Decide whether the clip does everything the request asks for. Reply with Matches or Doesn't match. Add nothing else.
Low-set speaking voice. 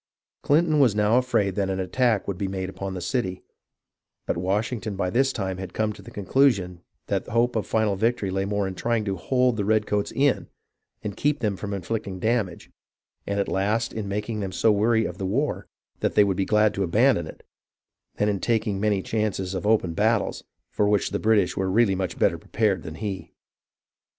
Matches